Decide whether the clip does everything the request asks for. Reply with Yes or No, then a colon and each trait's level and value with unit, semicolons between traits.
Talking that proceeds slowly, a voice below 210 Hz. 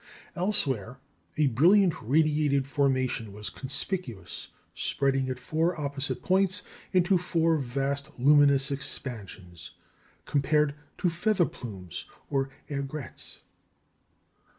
Yes: slow, 95 wpm; medium, 140 Hz